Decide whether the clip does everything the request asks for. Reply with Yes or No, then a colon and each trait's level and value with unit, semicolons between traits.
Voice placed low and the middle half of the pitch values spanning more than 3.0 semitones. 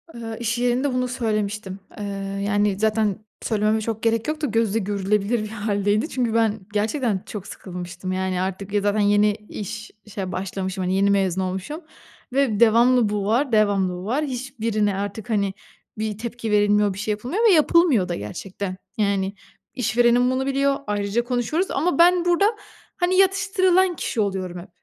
No: high, 215 Hz; average, 3.7 semitones